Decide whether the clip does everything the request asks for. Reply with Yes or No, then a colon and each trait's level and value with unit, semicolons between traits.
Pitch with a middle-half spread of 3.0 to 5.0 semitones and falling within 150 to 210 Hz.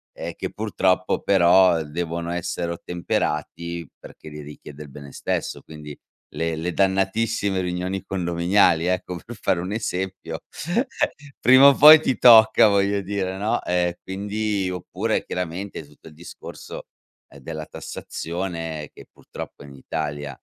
No: average, 3.3 semitones; very low, 90 Hz